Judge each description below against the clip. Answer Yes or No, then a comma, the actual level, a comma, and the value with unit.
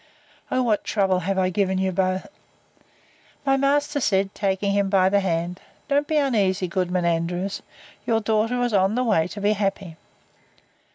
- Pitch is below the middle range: No, high, 195 Hz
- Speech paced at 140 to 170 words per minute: Yes, average, 165 wpm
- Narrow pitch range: No, average, 3.1 semitones